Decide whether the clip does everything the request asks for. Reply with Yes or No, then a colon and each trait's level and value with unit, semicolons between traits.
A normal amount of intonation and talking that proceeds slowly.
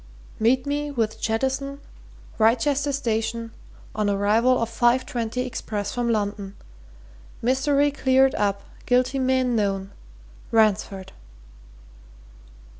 Yes: average, 3.4 semitones; slow, 100 wpm